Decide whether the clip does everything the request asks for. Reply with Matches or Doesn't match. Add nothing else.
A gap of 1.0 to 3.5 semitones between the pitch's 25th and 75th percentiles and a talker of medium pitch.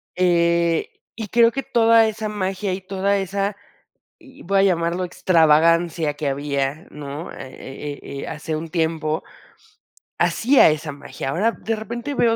Doesn't match